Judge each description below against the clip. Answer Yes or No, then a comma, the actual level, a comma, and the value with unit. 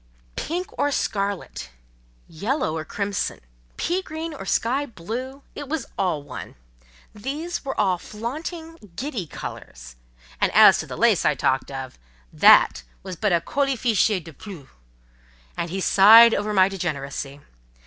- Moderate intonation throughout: No, wide, 8.3 semitones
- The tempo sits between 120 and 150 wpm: Yes, average, 140 wpm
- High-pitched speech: Yes, high, 210 Hz